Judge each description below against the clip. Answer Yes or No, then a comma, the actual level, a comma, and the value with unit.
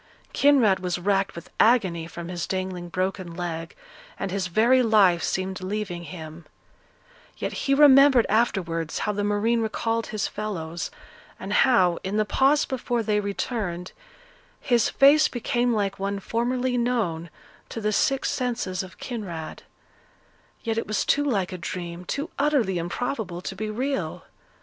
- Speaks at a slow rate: No, average, 150 wpm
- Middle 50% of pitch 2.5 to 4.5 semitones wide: No, average, 5.0 semitones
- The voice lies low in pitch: No, high, 205 Hz